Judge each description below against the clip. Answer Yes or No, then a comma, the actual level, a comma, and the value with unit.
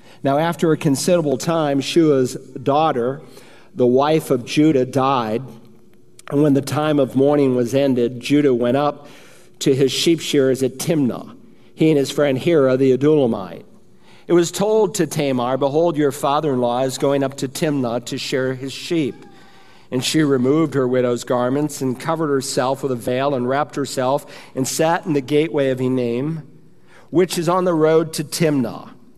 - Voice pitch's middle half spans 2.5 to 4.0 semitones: Yes, average, 3.1 semitones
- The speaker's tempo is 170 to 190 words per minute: Yes, average, 175 wpm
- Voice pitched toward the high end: No, medium, 140 Hz